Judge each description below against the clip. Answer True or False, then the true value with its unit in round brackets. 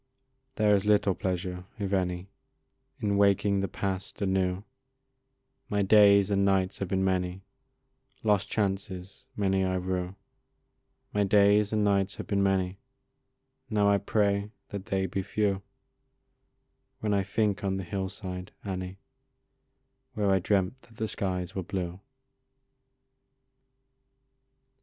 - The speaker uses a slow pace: True (130 wpm)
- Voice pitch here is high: False (95 Hz)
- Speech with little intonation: True (1.5 semitones)